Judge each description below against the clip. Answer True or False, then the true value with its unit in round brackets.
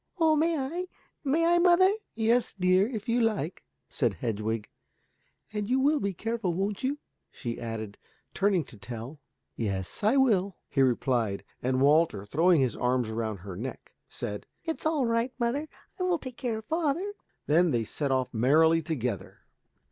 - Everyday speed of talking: True (165 wpm)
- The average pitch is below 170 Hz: False (185 Hz)